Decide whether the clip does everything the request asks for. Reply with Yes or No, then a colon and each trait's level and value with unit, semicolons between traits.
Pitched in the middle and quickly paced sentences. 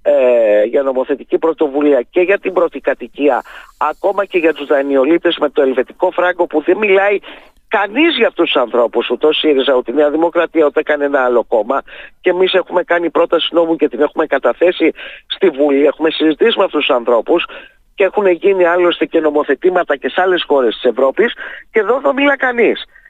Yes: medium, 165 Hz; fast, 180 wpm